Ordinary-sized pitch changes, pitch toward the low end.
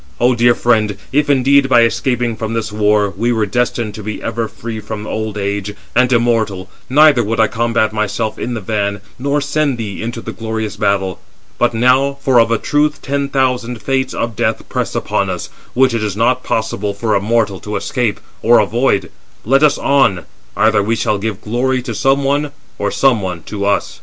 Yes: average, 3.2 semitones; low, 115 Hz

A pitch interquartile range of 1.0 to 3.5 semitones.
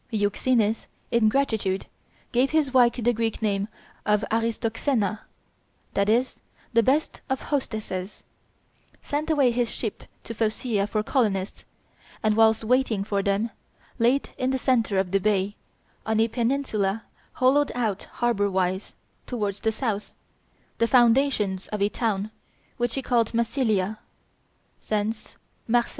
Yes: average, 3.2 semitones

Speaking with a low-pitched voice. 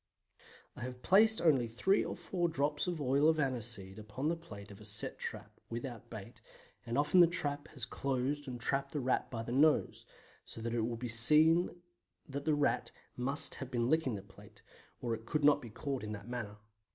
Yes: low, 130 Hz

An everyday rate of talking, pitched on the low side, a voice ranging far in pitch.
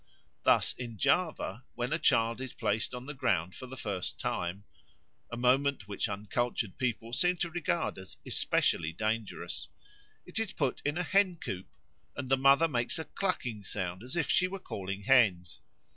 Yes: average, 175 wpm; low, 125 Hz; wide, 6.3 semitones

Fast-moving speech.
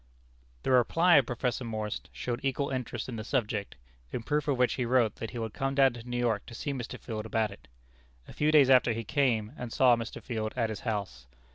Yes: fast, 230 wpm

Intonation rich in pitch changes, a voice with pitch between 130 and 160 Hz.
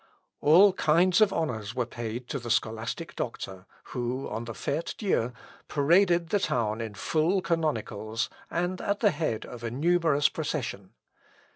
Yes: wide, 7.0 semitones; medium, 140 Hz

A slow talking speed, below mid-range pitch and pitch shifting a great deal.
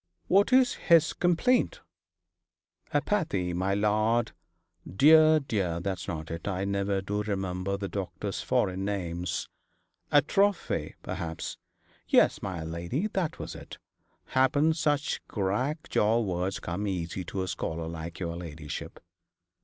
Yes: slow, 125 wpm; low, 100 Hz; wide, 8.7 semitones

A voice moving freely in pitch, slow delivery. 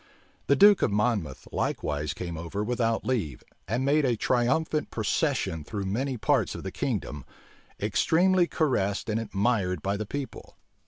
No: wide, 5.7 semitones; average, 150 wpm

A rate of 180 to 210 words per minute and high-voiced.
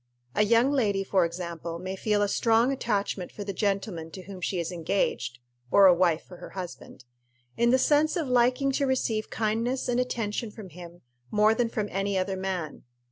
Yes: average, 190 wpm; high, 200 Hz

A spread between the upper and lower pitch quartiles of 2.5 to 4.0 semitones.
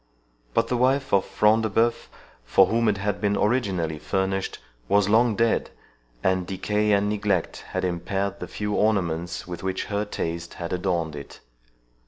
Yes: average, 2.9 semitones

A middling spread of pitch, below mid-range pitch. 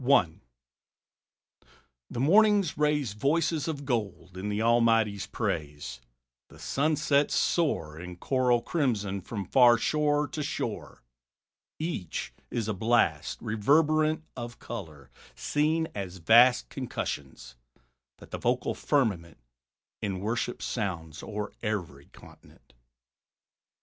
No: wide, 7.7 semitones; low, 115 Hz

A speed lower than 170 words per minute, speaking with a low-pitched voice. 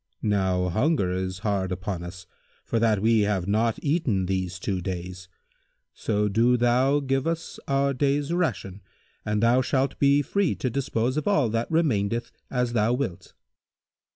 Yes: average, 155 wpm; low, 115 Hz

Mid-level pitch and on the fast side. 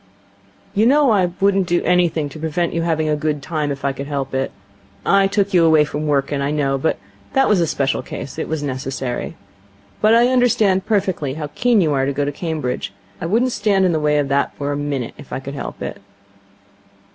Yes: medium, 155 Hz; fast, 215 wpm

